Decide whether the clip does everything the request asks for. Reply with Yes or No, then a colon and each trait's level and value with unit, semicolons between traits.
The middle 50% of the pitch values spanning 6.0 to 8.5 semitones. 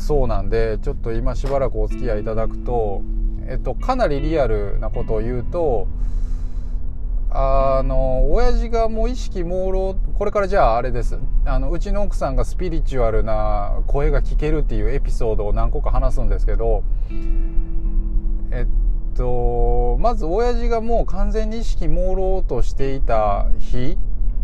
No: wide, 5.6 semitones